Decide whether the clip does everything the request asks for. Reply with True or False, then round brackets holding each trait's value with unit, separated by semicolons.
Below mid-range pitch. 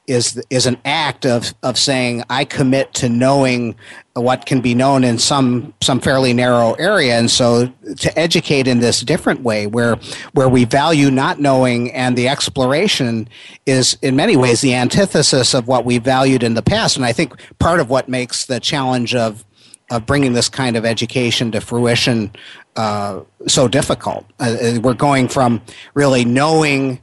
True (125 Hz)